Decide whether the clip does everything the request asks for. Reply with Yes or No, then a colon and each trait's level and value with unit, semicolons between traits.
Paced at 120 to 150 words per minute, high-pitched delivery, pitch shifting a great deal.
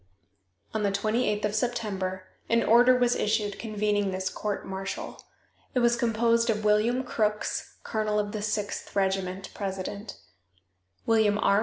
No: average, 140 wpm; high, 210 Hz; narrow, 2.4 semitones